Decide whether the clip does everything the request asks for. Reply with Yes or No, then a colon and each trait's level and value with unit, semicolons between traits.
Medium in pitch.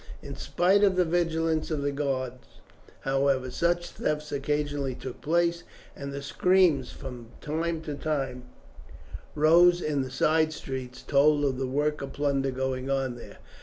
Yes: medium, 145 Hz